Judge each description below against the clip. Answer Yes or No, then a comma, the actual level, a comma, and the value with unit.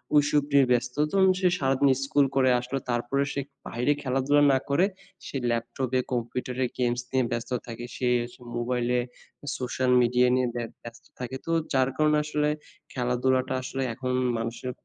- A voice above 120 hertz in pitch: Yes, low, 130 Hz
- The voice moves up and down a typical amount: No, narrow, 2.2 semitones